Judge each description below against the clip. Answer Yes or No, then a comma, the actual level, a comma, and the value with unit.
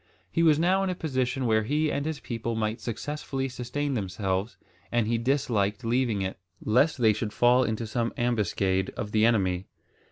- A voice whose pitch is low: Yes, low, 120 Hz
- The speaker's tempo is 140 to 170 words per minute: No, average, 180 wpm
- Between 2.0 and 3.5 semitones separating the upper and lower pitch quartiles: No, average, 4.0 semitones